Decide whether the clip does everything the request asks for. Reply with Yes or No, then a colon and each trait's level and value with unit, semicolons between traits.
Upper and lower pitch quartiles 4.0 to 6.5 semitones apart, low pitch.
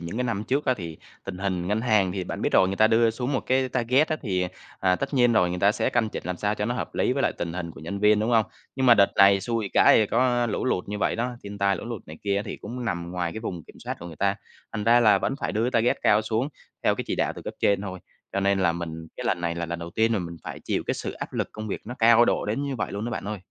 Yes: average, 4.3 semitones; low, 105 Hz